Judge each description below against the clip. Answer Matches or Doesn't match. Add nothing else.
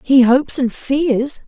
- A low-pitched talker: Doesn't match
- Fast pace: Doesn't match